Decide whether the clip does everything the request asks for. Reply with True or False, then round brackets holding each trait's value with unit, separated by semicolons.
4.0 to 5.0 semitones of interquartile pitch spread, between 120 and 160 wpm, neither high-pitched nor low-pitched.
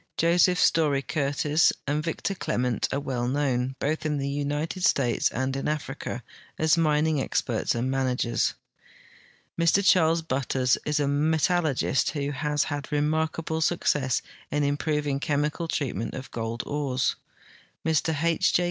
False (2.9 semitones; 145 wpm; 145 Hz)